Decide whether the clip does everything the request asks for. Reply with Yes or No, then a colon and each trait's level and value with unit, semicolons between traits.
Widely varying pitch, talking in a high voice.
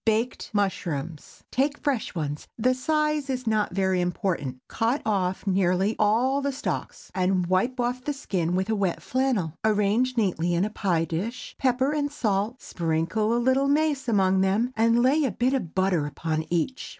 Yes: wide, 5.9 semitones; high, 215 Hz